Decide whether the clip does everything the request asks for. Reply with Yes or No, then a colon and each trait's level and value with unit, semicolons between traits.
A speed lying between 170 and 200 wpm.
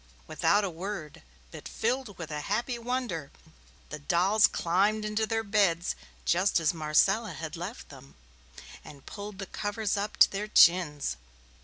No: average, 150 wpm